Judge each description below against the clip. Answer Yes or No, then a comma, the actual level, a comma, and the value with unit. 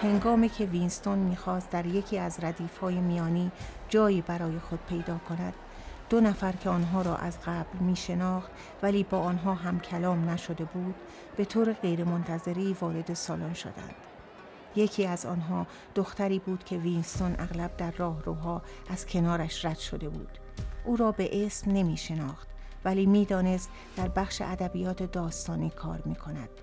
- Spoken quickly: No, average, 145 wpm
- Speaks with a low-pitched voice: No, medium, 180 Hz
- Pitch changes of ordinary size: No, narrow, 2.0 semitones